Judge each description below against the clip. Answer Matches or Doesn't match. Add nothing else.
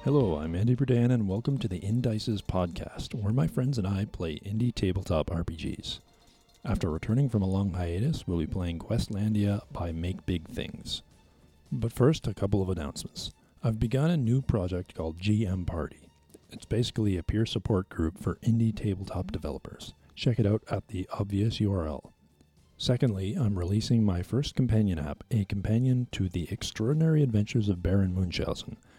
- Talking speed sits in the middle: Matches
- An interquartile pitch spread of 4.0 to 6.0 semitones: Matches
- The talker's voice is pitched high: Doesn't match